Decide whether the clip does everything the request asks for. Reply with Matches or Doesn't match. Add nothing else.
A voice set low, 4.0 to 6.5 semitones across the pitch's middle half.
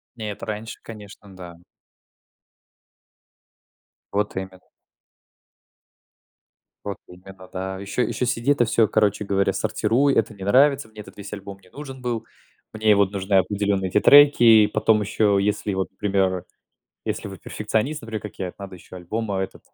Doesn't match